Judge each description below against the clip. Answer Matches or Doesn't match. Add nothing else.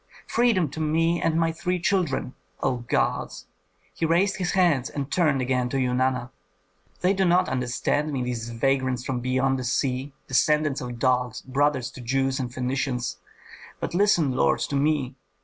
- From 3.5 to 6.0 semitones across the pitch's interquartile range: Matches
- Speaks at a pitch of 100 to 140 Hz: Matches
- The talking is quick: Doesn't match